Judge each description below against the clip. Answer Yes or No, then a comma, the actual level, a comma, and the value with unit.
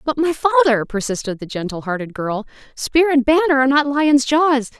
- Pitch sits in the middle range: No, very high, 255 Hz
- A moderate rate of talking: Yes, average, 190 wpm